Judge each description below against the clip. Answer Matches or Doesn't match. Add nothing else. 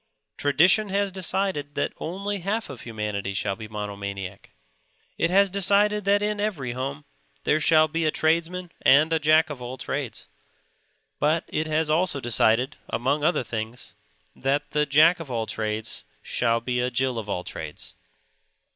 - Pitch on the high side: Doesn't match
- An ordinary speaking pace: Matches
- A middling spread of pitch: Doesn't match